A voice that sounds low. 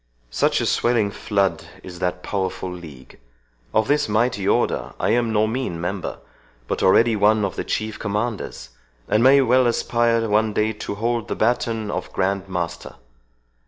Yes: low, 105 Hz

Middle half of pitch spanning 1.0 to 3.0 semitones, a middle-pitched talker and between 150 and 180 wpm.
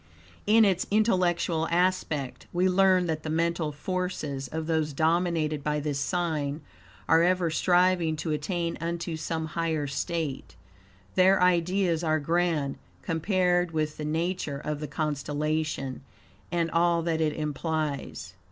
No: narrow, 2.6 semitones; medium, 165 Hz; slow, 135 wpm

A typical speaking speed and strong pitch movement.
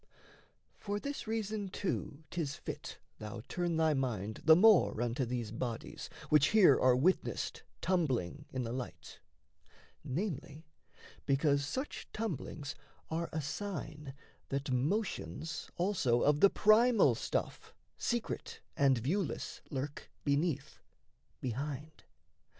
No: slow, 115 wpm; wide, 6.1 semitones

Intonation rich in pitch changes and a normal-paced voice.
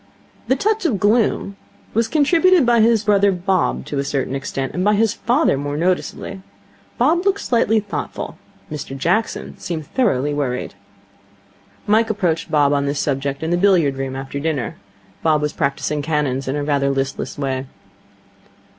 Yes: wide, 7.7 semitones; average, 160 wpm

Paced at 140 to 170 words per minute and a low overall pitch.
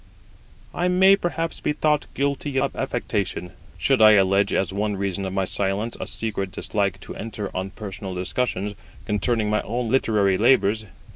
Yes: average, 160 wpm; low, 105 Hz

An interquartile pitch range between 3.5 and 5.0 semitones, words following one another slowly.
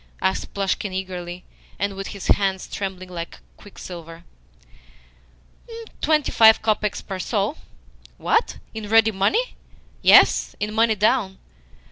No: average, 2.7 semitones; slow, 115 wpm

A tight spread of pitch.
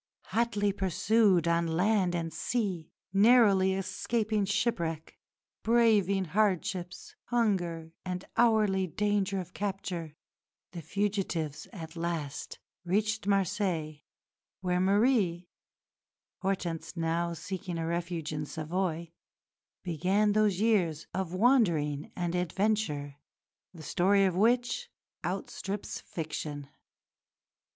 No: average, 3.7 semitones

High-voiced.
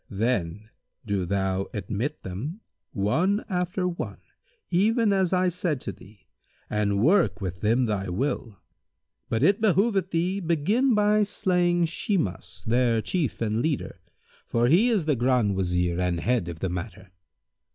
No: low, 125 Hz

